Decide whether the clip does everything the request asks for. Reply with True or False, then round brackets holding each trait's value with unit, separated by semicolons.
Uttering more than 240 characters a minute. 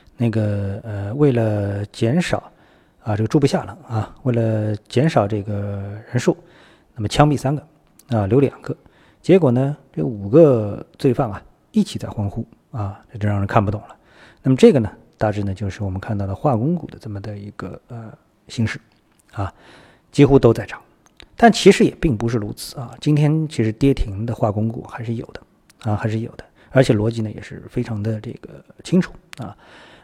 True (265 characters per minute)